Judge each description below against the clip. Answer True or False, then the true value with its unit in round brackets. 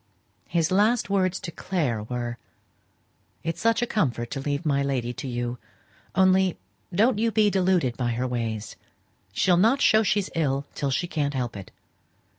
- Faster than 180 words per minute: False (165 wpm)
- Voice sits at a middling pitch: True (155 Hz)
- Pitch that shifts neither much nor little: False (7.6 semitones)